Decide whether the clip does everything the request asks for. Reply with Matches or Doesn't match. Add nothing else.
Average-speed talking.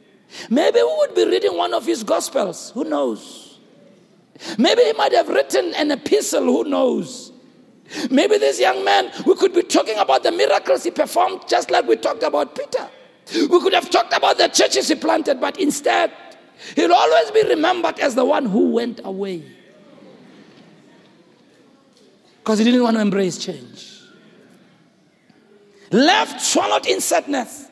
Matches